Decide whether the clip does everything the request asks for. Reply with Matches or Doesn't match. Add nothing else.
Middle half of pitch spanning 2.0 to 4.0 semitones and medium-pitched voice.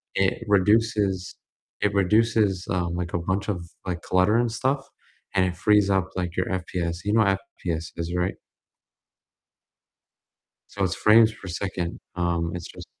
Doesn't match